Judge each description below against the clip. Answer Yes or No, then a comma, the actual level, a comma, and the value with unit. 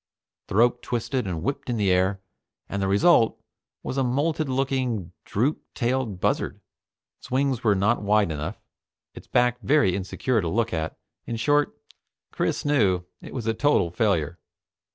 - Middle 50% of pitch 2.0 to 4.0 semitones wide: No, average, 5.3 semitones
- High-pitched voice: No, low, 115 Hz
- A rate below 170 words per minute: Yes, average, 160 wpm